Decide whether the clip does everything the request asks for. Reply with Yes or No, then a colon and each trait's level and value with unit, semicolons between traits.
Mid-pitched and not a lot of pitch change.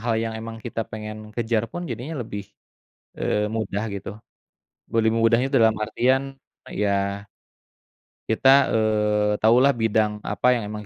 No: low, 110 Hz; narrow, 1.9 semitones